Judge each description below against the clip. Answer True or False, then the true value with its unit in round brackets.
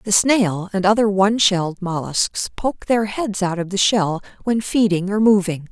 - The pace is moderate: True (190 wpm)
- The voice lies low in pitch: False (200 Hz)